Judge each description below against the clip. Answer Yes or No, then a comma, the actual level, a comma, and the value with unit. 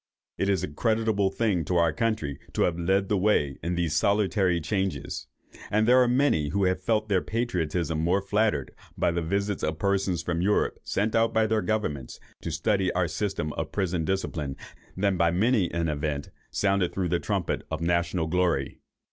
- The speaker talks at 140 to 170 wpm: No, average, 185 wpm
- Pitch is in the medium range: No, very low, 90 Hz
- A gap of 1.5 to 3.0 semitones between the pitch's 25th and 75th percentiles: No, average, 3.7 semitones